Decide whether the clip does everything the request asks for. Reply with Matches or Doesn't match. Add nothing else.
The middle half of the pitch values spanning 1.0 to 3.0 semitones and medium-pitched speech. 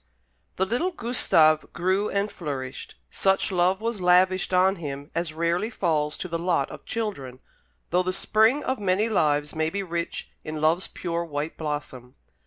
Doesn't match